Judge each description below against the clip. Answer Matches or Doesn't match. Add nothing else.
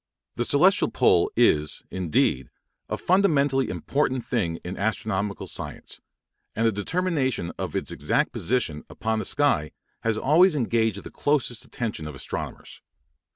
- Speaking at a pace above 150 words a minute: Doesn't match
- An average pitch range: Doesn't match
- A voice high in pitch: Doesn't match